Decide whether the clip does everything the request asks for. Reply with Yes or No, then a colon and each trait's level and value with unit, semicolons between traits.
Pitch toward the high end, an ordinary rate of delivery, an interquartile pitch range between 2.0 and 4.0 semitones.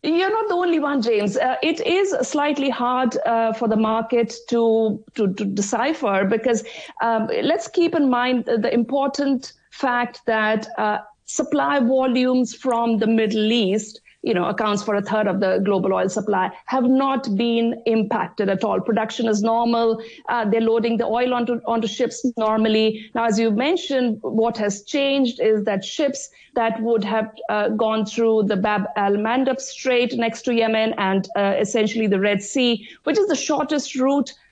Yes: high, 230 Hz; average, 175 wpm; average, 2.9 semitones